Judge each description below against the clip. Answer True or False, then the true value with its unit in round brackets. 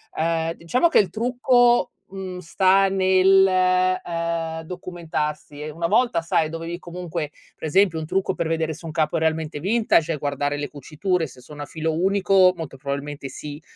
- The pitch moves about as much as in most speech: True (3.3 semitones)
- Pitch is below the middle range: False (170 Hz)